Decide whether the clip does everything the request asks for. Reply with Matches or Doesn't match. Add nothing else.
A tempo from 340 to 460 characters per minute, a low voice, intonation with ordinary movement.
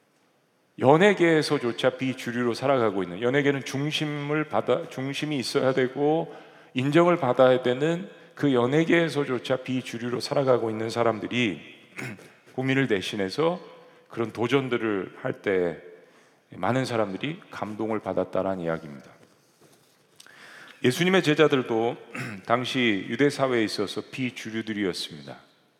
Doesn't match